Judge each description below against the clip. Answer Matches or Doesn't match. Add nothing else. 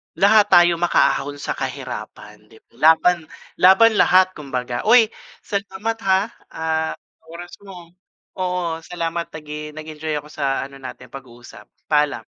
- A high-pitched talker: Doesn't match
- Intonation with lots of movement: Doesn't match